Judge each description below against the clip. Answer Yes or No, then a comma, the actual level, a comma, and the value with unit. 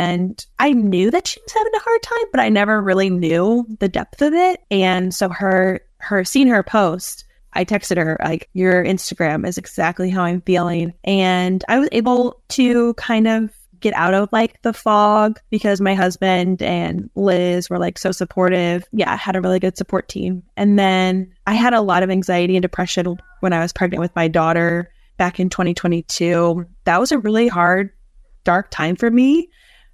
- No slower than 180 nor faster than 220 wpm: Yes, average, 190 wpm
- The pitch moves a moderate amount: Yes, average, 3.4 semitones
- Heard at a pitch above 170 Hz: Yes, high, 190 Hz